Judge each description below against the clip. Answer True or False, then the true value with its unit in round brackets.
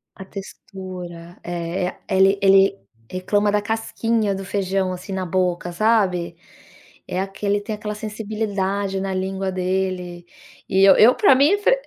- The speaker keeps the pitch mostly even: True (2.1 semitones)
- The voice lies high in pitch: True (195 Hz)